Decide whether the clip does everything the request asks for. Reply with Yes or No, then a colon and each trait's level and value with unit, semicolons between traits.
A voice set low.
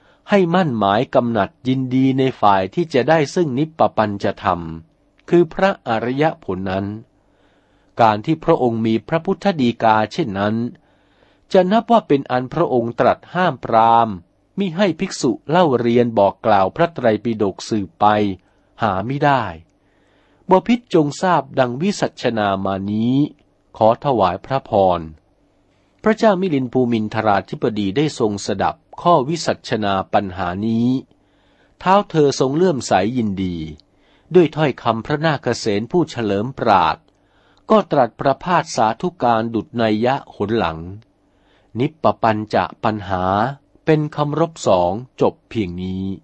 Yes: low, 120 Hz